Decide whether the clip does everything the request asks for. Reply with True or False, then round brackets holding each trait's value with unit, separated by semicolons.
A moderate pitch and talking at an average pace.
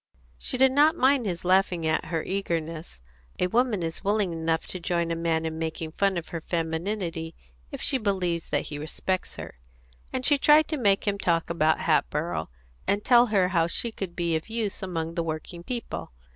True (175 Hz; 195 wpm)